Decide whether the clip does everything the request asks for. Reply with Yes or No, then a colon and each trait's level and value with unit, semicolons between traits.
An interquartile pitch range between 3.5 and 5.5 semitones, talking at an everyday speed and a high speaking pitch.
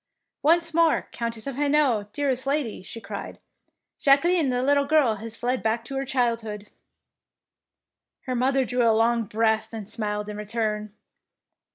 Yes: average, 4.0 semitones; average, 160 wpm; high, 235 Hz